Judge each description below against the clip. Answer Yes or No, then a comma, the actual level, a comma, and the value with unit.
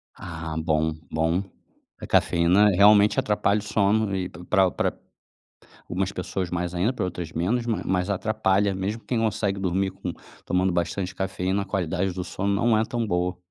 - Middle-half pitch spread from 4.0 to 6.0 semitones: No, average, 2.7 semitones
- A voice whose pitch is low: Yes, very low, 95 Hz